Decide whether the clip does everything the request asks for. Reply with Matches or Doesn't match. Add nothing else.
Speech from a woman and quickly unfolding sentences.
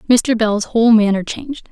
Doesn't match